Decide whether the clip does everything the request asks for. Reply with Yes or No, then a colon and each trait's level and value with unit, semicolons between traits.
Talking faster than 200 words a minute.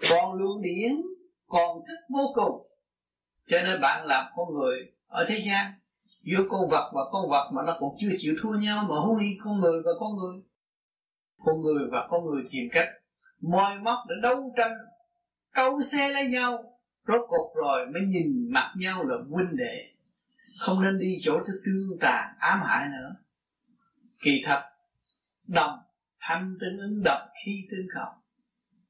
No: average, 170 wpm